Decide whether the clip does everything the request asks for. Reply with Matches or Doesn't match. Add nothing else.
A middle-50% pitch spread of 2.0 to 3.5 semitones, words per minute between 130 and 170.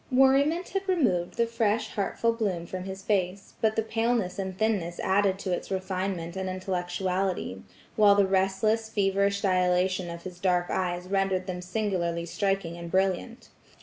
Matches